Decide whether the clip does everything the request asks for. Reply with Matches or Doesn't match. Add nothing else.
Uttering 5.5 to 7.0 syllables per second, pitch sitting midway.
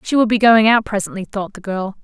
Doesn't match